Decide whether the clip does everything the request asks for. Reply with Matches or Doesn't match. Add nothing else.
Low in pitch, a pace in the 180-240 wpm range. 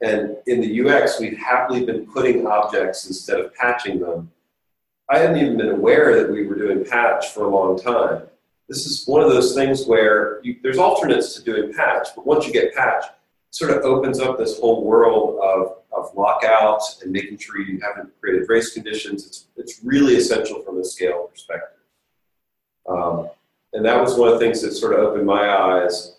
Matches